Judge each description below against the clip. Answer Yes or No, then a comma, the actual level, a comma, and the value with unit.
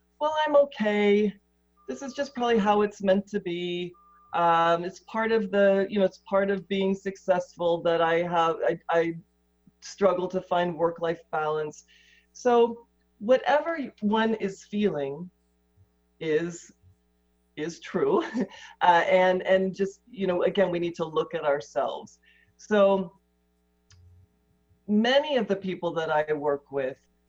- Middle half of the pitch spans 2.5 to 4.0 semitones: No, average, 5.3 semitones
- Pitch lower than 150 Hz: No, medium, 175 Hz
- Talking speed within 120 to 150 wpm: Yes, average, 145 wpm